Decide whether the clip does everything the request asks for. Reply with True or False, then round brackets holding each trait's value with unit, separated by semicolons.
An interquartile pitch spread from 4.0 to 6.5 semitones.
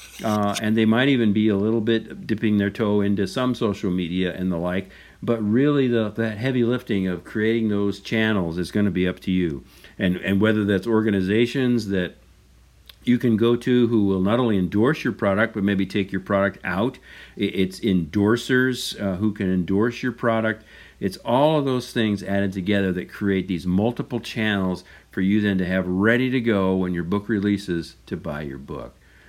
False (3.3 semitones)